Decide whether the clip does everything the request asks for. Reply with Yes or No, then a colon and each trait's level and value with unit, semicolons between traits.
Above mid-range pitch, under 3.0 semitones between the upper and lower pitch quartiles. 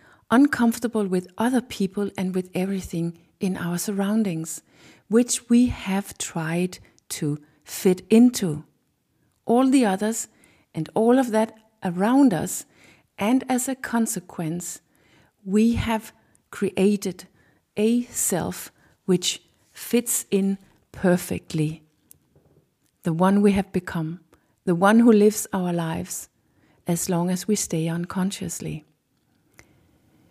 No: high, 195 Hz; average, 4.2 semitones